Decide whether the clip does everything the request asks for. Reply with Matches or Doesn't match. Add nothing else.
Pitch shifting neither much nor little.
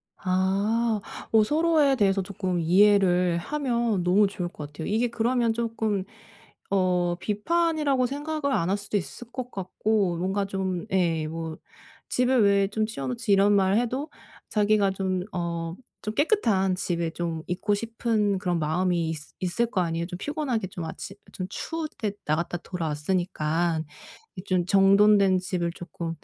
Matches